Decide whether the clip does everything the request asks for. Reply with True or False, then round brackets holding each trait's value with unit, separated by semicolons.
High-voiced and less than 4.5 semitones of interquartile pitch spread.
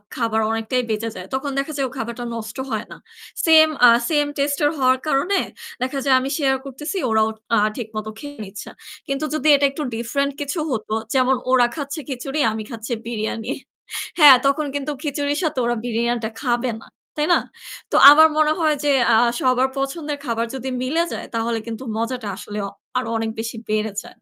True (260 Hz; 4.0 semitones)